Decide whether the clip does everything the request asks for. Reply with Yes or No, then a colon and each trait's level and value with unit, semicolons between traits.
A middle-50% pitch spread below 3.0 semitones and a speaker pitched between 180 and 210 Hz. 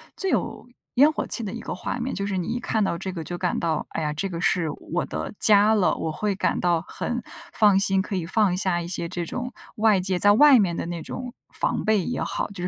No: average, 4.0 semitones; high, 195 Hz